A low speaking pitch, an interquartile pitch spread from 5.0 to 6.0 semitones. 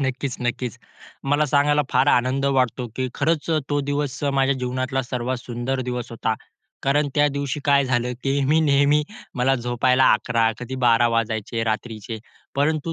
No: low, 130 Hz; average, 2.7 semitones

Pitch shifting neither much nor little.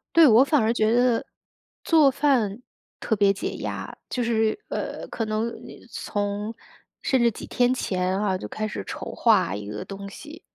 Yes: average, 4.0 semitones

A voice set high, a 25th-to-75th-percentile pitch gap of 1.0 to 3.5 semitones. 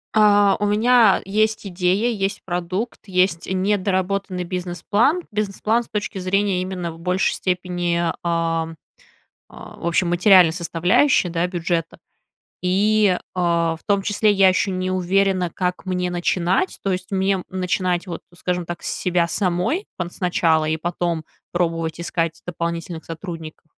No: medium, 180 Hz; narrow, 2.4 semitones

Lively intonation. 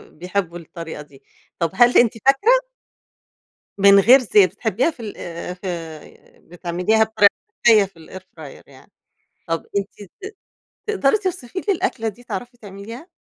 Yes: wide, 5.7 semitones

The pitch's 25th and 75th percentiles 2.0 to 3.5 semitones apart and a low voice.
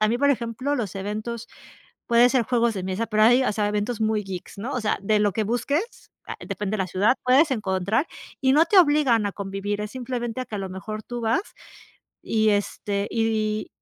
No: average, 3.1 semitones; high, 220 Hz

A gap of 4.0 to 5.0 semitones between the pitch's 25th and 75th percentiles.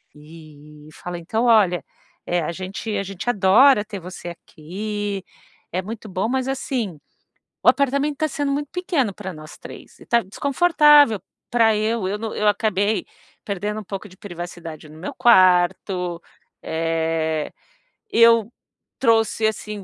Yes: average, 4.7 semitones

